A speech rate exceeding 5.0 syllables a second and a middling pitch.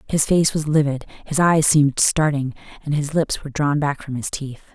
Yes: 5.3 syllables/s; medium, 145 Hz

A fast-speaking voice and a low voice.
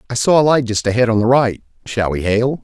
Yes: fast, 250 wpm; low, 120 Hz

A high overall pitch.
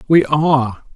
No: medium, 145 Hz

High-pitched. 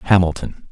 No: very low, 85 Hz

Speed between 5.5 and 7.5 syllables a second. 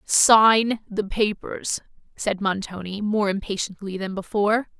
No: 4.0 syllables/s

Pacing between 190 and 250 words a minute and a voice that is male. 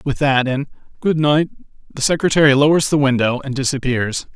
No: average, 165 wpm; male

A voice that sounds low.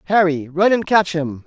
No: medium, 175 Hz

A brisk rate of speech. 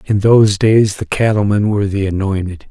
No: average, 180 wpm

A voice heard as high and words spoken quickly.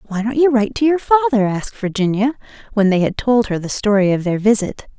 Yes: high, 225 Hz; fast, 230 wpm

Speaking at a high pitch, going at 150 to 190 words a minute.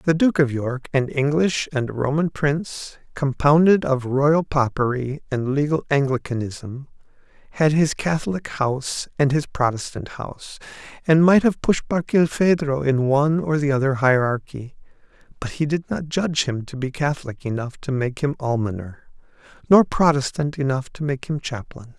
No: medium, 140 Hz; average, 155 wpm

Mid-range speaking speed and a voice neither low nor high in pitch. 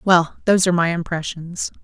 Yes: average, 165 wpm; medium, 175 Hz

